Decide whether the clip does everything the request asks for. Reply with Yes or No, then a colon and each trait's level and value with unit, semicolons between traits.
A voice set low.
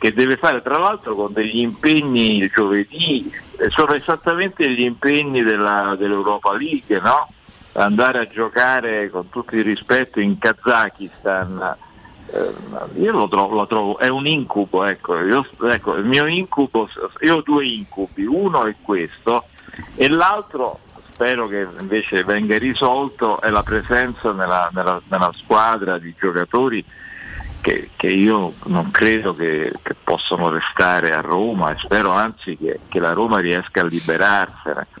Yes: low, 110 Hz